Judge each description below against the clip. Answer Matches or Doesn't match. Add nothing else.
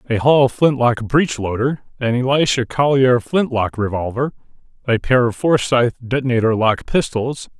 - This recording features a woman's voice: Doesn't match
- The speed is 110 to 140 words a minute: Matches